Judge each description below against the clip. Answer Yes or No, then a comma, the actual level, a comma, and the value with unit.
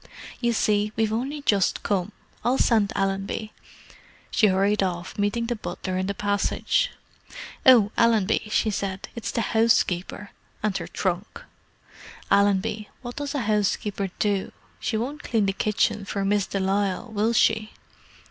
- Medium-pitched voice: No, high, 210 Hz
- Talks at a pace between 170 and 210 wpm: No, average, 150 wpm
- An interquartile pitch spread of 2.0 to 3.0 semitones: Yes, narrow, 2.4 semitones